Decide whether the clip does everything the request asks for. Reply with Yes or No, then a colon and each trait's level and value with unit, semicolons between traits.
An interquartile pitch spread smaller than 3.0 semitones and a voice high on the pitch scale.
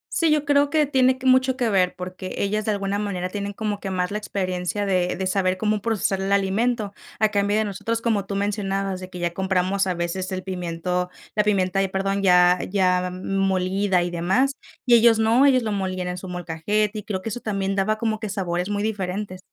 Yes: narrow, 2.6 semitones; high, 195 Hz